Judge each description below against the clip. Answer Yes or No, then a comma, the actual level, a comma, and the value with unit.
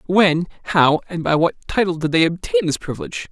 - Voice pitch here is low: No, medium, 165 Hz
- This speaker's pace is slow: No, average, 200 wpm